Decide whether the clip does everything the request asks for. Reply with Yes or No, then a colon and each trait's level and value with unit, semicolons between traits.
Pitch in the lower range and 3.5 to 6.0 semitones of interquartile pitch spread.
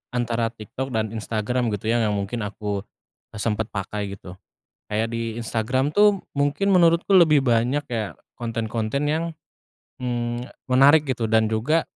Yes: low, 115 Hz; average, 4.2 semitones